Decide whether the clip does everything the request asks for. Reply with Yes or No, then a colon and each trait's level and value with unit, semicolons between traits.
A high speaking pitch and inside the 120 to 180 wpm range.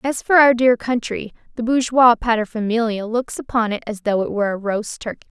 No: high, 230 Hz; average, 200 wpm